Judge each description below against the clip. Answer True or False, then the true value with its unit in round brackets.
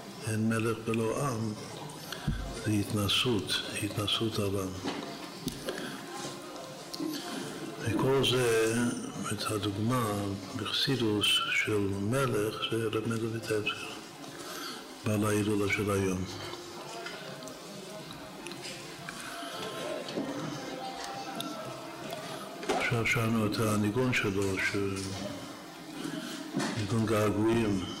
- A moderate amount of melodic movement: False (2.0 semitones)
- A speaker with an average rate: False (60 wpm)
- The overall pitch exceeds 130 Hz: False (105 Hz)